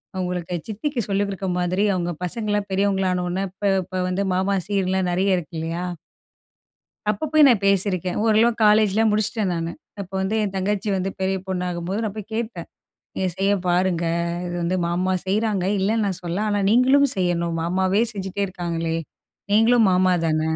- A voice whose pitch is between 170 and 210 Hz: Yes, high, 190 Hz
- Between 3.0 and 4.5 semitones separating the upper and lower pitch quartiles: No, narrow, 2.6 semitones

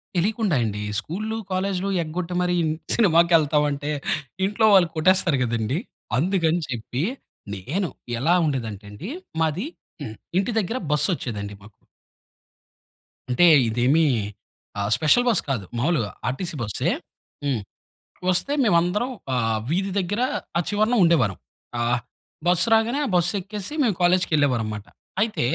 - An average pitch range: No, wide, 7.3 semitones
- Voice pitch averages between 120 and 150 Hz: No, medium, 165 Hz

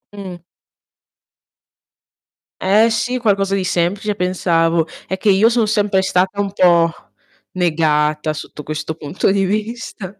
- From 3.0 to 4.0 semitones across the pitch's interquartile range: Yes, average, 3.6 semitones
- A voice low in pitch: No, high, 190 Hz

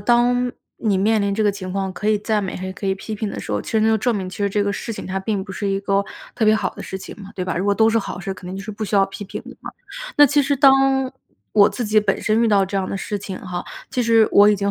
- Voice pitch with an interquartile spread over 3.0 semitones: No, narrow, 2.4 semitones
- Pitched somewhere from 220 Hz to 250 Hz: No, high, 205 Hz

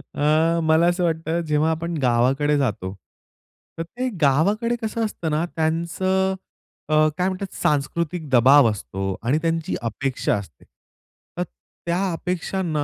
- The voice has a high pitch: No, medium, 160 Hz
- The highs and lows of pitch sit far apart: No, average, 4.1 semitones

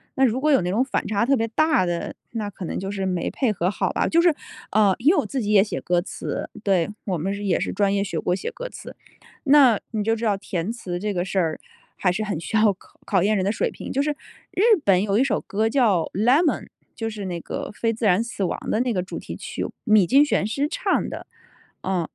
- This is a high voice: Yes, high, 210 Hz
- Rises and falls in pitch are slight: No, average, 4.0 semitones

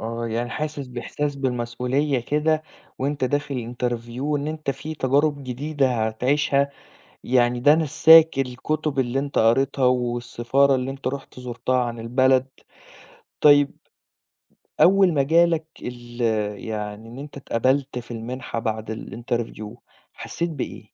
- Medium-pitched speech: No, low, 130 Hz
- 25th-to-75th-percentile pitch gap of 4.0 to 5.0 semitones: No, average, 3.2 semitones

